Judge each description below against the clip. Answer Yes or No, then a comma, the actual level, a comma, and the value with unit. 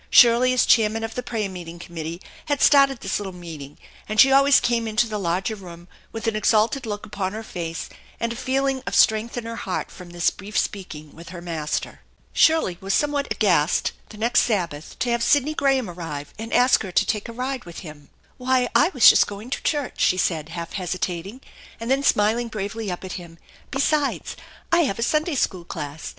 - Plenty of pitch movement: Yes, wide, 6.2 semitones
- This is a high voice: Yes, high, 215 Hz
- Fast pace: Yes, fast, 210 wpm